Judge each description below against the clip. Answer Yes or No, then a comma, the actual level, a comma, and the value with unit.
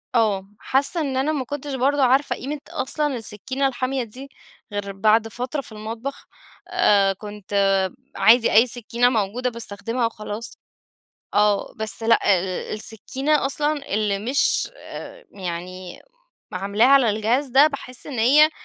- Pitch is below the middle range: No, high, 235 Hz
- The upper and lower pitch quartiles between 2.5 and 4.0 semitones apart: No, average, 4.5 semitones